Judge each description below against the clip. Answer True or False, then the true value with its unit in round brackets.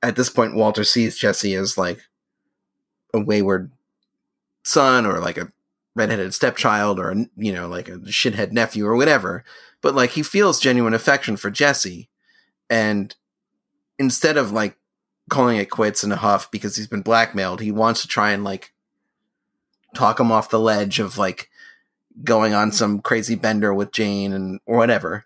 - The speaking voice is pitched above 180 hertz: False (110 Hz)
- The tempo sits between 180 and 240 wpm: False (165 wpm)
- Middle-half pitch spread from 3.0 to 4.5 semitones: False (2.4 semitones)